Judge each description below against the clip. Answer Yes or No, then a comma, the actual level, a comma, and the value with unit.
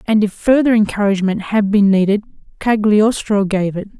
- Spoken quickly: No, average, 150 wpm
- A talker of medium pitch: No, high, 210 Hz